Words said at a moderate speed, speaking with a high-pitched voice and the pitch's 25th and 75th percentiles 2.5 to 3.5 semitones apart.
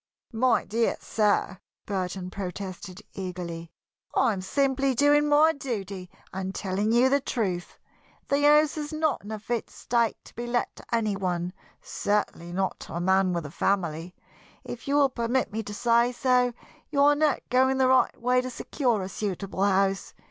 No: average, 175 wpm; high, 220 Hz; wide, 5.4 semitones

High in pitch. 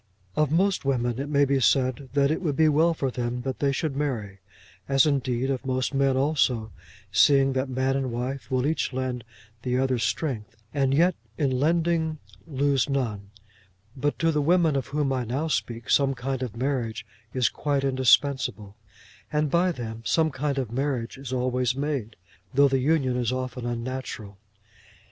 No: low, 135 Hz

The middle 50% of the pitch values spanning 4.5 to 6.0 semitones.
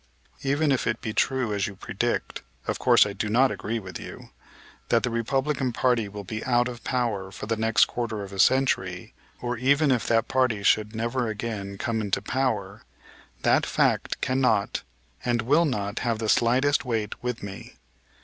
No: average, 3.4 semitones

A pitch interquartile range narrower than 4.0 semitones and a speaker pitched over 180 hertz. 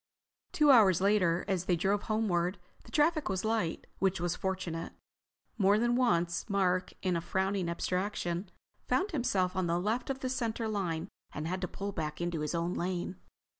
Yes: average, 3.6 semitones; high, 190 Hz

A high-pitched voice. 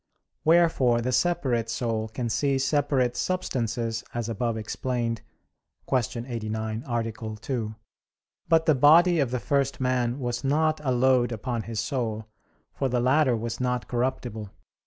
No: low, 125 Hz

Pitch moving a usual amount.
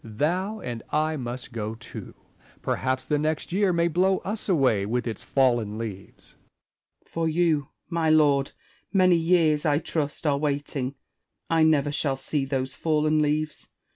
Yes: average, 3.9 semitones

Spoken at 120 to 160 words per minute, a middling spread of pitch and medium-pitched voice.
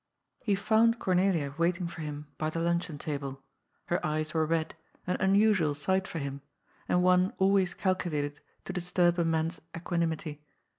Yes: average, 155 wpm; average, 3.0 semitones; medium, 170 Hz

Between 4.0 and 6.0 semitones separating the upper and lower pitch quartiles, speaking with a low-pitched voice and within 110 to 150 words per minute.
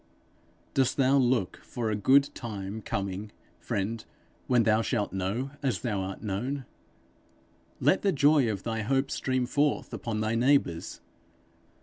Yes: average, 4.4 semitones; low, 115 Hz; average, 140 wpm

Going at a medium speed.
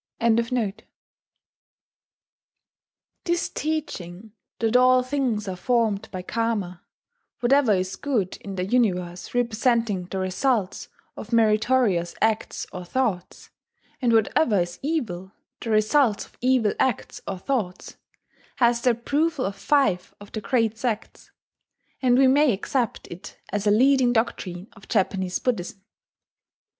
No: slow, 130 wpm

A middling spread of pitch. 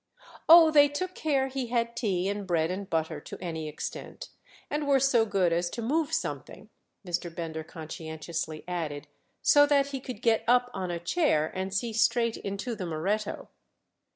No: wide, 7.6 semitones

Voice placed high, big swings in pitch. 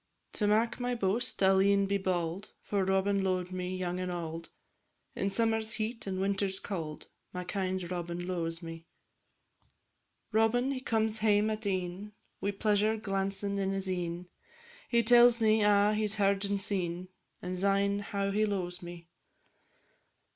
No: high, 195 Hz; narrow, 2.5 semitones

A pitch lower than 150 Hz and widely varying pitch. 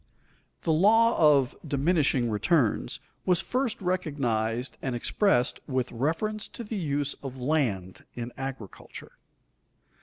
Yes: medium, 140 Hz; wide, 6.5 semitones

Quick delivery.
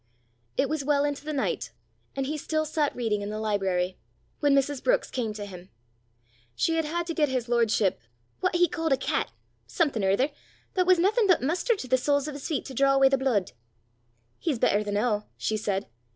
Yes: fast, 210 wpm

